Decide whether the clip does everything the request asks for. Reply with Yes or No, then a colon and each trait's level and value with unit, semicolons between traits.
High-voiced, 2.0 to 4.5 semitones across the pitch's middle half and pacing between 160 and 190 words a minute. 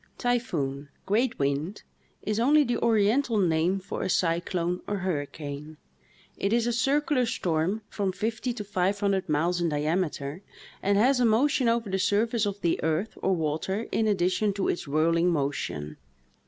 No: high, 195 Hz; wide, 5.6 semitones; average, 170 wpm